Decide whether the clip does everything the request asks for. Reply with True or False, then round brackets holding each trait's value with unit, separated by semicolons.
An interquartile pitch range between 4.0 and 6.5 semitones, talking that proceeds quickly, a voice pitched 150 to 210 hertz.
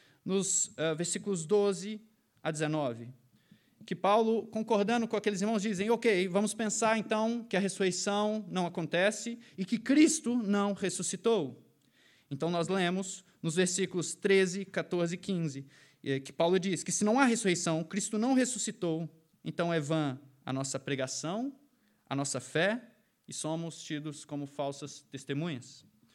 False (5.2 semitones; 140 wpm; 190 Hz)